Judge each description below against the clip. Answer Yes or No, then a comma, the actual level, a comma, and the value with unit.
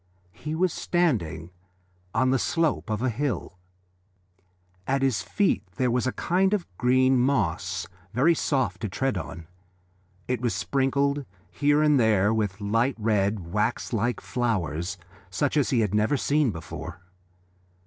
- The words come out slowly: No, average, 145 wpm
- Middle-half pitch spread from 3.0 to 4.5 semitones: No, average, 5.3 semitones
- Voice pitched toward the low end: Yes, low, 125 Hz